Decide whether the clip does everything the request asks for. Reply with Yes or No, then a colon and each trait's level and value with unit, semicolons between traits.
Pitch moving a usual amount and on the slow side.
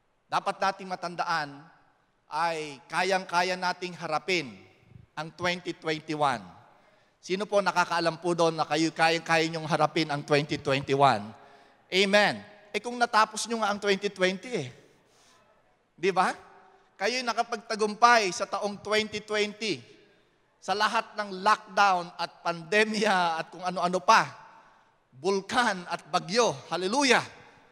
Yes: average, 4.3 semitones; slow, 115 wpm